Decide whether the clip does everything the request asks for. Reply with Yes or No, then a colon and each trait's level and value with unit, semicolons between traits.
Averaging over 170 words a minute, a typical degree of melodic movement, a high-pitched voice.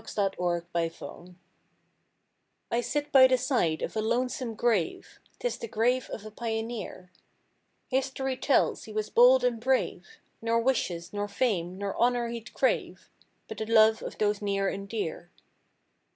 No: average, 155 wpm; average, 3.9 semitones; high, 225 Hz